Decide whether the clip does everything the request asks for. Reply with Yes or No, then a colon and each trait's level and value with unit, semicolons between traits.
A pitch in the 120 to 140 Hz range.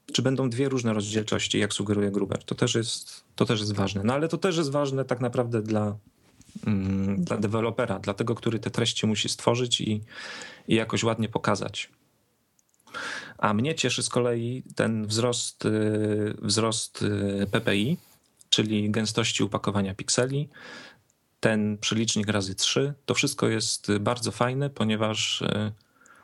No: low, 110 Hz